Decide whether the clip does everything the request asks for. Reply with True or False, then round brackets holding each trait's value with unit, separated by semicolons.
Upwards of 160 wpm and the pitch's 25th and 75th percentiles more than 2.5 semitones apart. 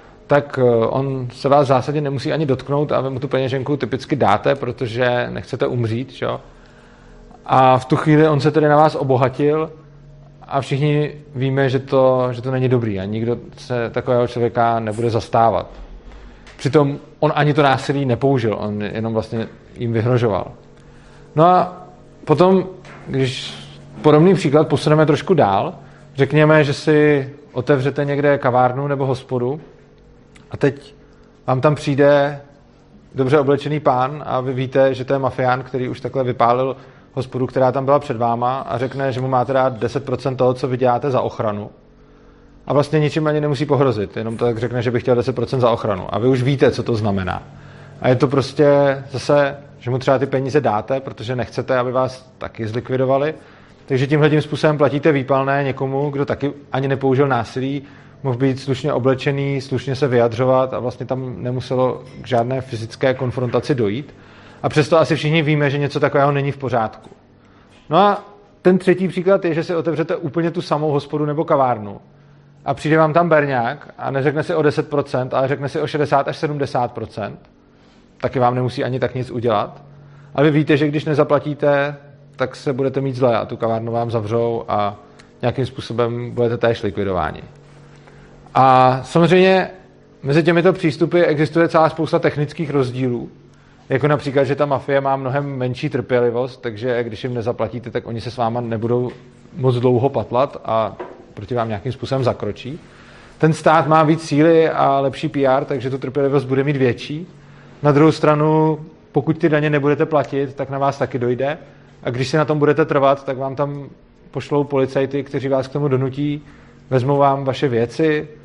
True (170 wpm; 2.9 semitones)